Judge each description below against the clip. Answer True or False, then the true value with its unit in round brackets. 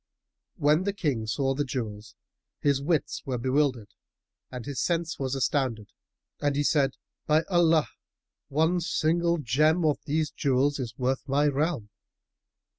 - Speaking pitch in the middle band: True (145 Hz)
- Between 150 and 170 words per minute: False (140 wpm)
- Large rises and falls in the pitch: False (3.5 semitones)